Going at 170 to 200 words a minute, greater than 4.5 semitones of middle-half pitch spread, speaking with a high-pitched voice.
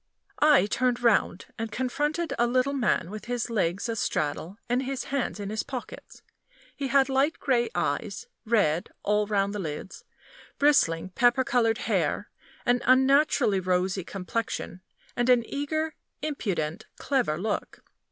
No: average, 140 wpm; average, 5.2 semitones; high, 235 Hz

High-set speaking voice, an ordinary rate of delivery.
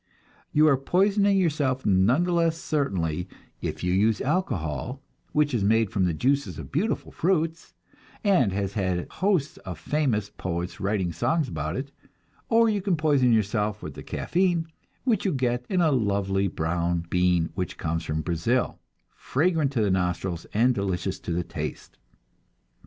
No: low, 115 Hz; average, 160 wpm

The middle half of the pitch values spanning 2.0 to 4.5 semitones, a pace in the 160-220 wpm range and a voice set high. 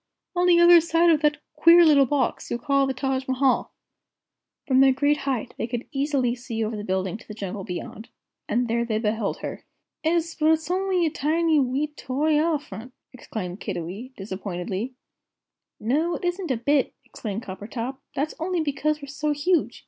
No: average, 5.3 semitones; average, 180 wpm; very high, 270 Hz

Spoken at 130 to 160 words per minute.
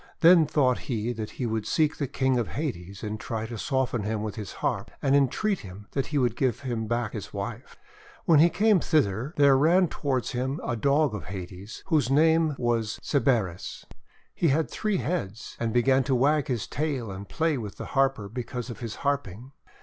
No: average, 195 wpm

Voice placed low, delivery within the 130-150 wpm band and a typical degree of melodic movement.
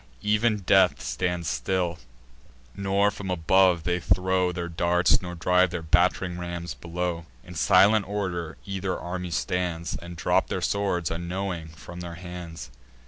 No: very low, 90 Hz; average, 140 wpm; narrow, 1.6 semitones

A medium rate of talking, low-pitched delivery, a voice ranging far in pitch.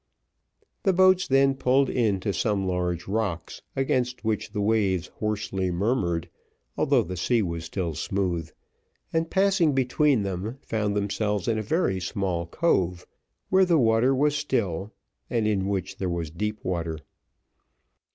Yes: average, 145 wpm; low, 105 Hz; wide, 5.9 semitones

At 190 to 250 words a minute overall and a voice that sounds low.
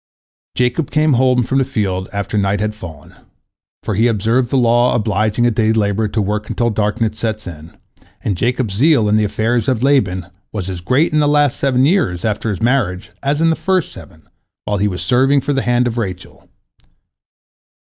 Yes: average, 195 wpm; low, 115 Hz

